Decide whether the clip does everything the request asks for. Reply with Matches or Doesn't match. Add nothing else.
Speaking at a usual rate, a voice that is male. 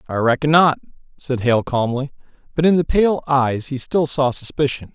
Matches